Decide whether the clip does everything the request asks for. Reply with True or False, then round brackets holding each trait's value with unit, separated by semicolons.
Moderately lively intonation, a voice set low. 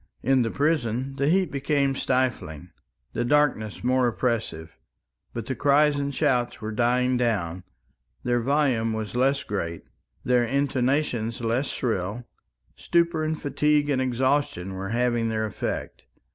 True (3.9 semitones; 125 Hz)